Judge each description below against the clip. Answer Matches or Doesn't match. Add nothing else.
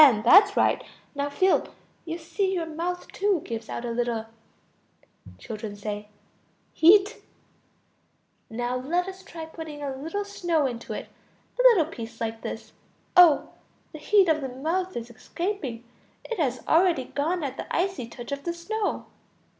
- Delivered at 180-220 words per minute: Doesn't match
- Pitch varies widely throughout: Matches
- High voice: Matches